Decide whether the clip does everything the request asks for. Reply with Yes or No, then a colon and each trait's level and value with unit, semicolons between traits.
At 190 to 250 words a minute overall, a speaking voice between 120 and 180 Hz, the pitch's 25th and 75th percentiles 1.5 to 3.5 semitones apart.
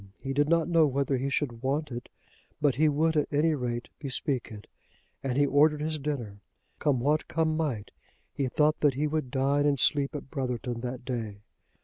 Yes: average, 195 wpm; medium, 140 Hz; average, 3.2 semitones